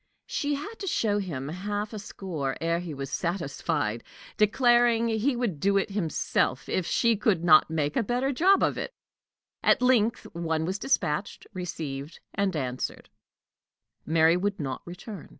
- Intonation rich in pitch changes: Yes, wide, 6.2 semitones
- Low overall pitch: No, high, 190 Hz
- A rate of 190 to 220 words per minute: No, average, 155 wpm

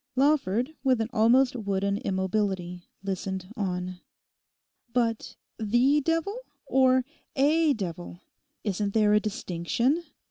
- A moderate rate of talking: No, slow, 105 wpm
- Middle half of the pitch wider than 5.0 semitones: Yes, wide, 5.4 semitones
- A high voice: Yes, high, 220 Hz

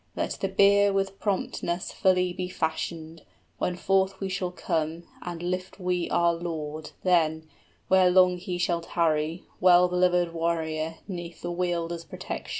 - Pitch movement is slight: Yes, narrow, 1.7 semitones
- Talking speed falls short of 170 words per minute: Yes, average, 150 wpm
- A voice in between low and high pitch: Yes, medium, 175 Hz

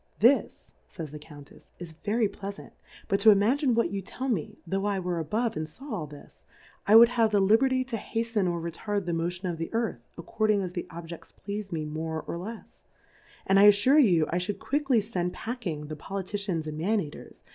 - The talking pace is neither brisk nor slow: No, fast, 210 wpm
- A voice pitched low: No, high, 195 Hz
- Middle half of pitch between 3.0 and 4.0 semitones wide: No, average, 4.9 semitones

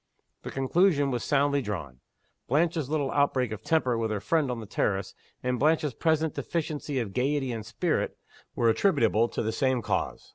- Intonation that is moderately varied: Yes, average, 4.7 semitones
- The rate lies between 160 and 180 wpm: Yes, average, 175 wpm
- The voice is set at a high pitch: No, low, 130 Hz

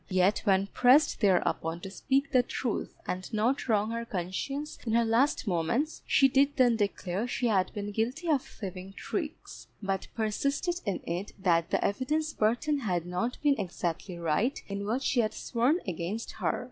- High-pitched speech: Yes, high, 220 Hz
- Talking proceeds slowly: No, average, 170 wpm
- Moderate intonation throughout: No, wide, 5.8 semitones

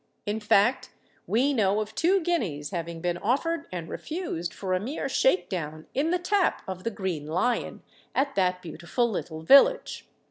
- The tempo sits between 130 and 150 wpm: No, average, 170 wpm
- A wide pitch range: Yes, wide, 7.8 semitones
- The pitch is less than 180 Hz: No, high, 205 Hz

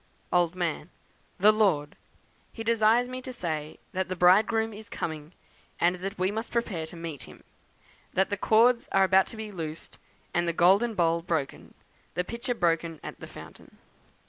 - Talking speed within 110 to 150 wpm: No, average, 170 wpm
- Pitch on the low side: No, medium, 185 Hz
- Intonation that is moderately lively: Yes, average, 4.7 semitones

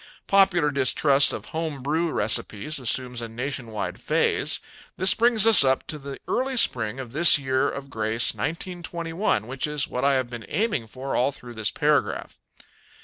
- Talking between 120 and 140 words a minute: No, average, 165 wpm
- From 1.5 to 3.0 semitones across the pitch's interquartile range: No, average, 5.2 semitones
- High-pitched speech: No, low, 135 Hz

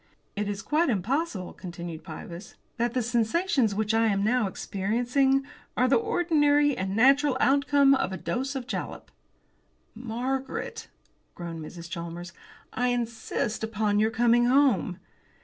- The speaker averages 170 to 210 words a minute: No, slow, 135 wpm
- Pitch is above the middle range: Yes, high, 235 Hz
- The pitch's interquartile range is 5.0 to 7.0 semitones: Yes, wide, 5.4 semitones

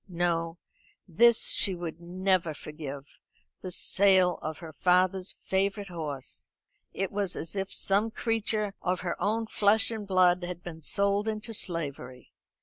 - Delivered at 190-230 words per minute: No, average, 145 wpm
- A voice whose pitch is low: No, medium, 185 Hz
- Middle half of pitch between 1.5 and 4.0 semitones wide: Yes, average, 3.1 semitones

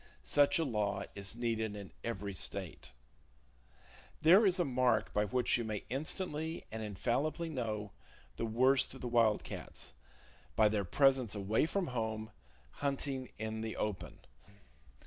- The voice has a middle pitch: No, low, 115 Hz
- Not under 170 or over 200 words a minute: No, average, 140 wpm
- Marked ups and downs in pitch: No, average, 4.6 semitones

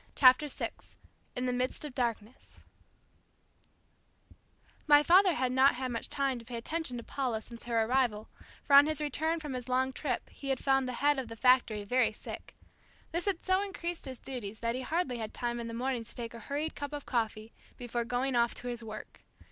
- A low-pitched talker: No, very high, 255 Hz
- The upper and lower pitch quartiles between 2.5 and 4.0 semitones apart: Yes, average, 3.3 semitones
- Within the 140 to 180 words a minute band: No, fast, 205 wpm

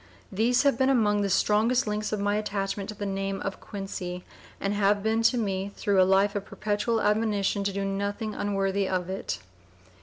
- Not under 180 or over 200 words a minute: Yes, average, 185 wpm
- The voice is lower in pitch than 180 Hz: No, high, 205 Hz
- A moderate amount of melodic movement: No, narrow, 1.6 semitones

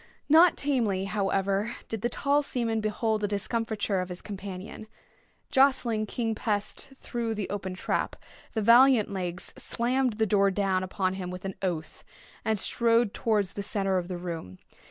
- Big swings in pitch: No, average, 3.4 semitones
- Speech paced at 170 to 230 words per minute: No, average, 160 wpm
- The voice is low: No, high, 210 Hz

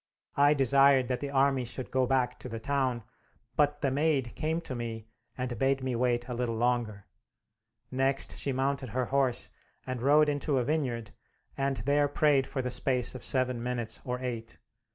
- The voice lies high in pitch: No, low, 130 Hz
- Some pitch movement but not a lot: No, narrow, 2.2 semitones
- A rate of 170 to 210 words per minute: Yes, average, 180 wpm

